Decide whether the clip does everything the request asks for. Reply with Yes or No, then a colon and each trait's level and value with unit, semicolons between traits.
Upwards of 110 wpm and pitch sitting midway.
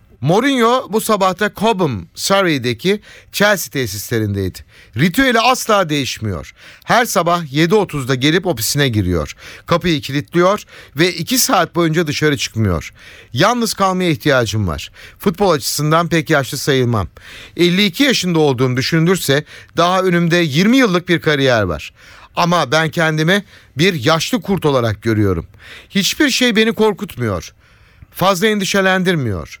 Yes: average, 120 wpm; medium, 160 Hz